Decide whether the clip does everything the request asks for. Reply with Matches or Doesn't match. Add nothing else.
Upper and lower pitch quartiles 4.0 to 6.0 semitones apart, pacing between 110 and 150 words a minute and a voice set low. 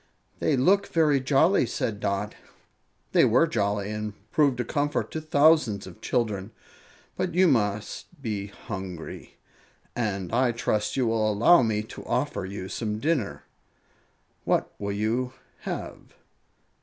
Matches